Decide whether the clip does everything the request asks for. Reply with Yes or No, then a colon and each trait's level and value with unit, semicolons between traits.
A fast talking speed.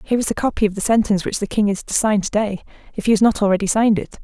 Yes: fast, 310 wpm